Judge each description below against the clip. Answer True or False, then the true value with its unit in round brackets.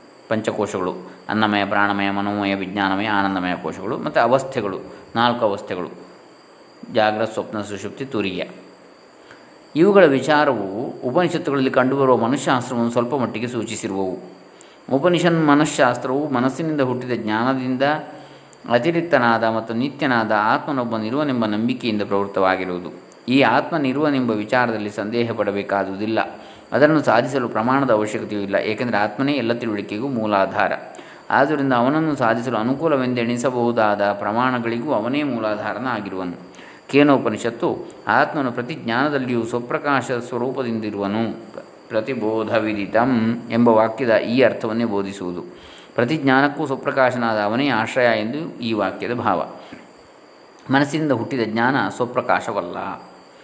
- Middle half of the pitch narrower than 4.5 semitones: True (4.1 semitones)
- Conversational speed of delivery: True (90 wpm)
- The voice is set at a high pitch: False (115 Hz)